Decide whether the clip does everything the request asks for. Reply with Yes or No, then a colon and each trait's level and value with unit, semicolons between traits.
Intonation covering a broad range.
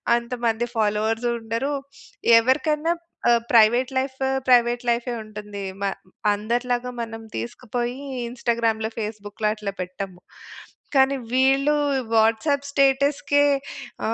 No: average, 3.1 semitones